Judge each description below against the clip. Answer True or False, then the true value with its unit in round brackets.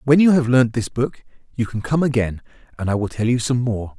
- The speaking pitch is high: False (120 Hz)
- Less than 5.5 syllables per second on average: False (5.6 syllables/s)